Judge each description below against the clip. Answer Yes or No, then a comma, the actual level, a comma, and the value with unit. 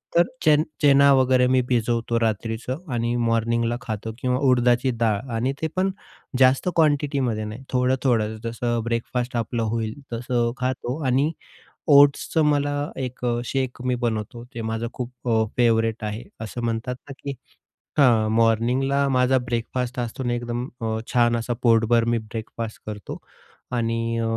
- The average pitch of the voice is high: No, low, 120 Hz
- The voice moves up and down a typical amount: No, narrow, 2.2 semitones